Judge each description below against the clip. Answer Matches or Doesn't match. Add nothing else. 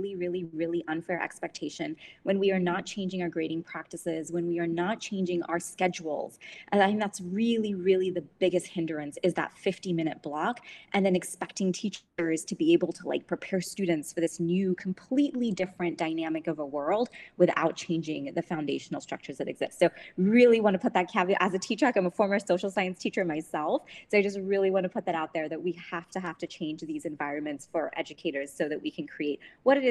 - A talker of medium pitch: Matches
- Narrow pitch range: Doesn't match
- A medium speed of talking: Doesn't match